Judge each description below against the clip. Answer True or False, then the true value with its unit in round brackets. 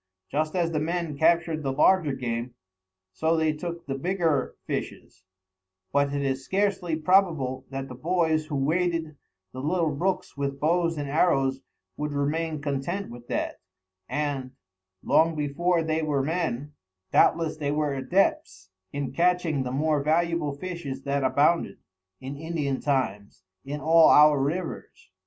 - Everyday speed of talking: True (145 wpm)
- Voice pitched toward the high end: False (150 Hz)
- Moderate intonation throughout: True (3.4 semitones)